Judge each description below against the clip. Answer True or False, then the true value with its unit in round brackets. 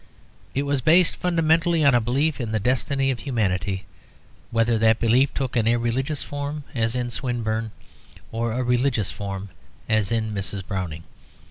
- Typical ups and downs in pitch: True (4.0 semitones)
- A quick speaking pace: False (155 wpm)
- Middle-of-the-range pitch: False (120 Hz)